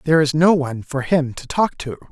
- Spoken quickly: Yes, fast, 255 wpm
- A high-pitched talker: No, medium, 145 Hz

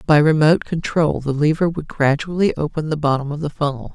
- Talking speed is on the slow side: No, average, 200 wpm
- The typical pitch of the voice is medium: Yes, medium, 150 Hz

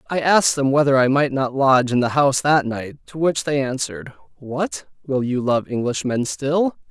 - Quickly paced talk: Yes, fast, 210 wpm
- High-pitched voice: No, low, 135 Hz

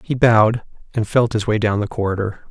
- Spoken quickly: Yes, fast, 215 wpm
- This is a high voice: No, low, 110 Hz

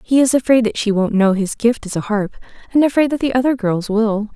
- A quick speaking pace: Yes, fast, 260 wpm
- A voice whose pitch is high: Yes, high, 225 Hz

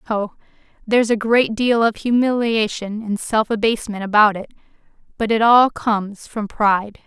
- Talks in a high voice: Yes, high, 220 Hz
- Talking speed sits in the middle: Yes, average, 155 wpm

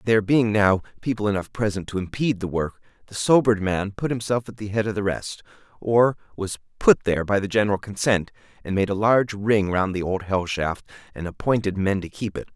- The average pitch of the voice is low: Yes, low, 105 Hz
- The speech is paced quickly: Yes, fast, 215 wpm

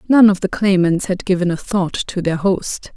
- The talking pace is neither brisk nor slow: No, fast, 225 wpm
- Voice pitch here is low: No, medium, 185 Hz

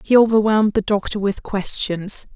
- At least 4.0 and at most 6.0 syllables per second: Yes, 5.0 syllables/s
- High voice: Yes, high, 205 Hz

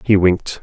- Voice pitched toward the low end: Yes, very low, 95 Hz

